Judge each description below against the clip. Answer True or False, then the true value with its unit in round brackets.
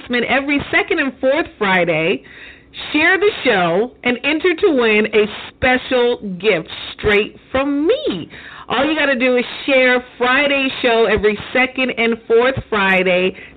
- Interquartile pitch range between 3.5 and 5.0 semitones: True (4.3 semitones)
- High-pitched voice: True (255 Hz)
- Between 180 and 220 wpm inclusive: False (140 wpm)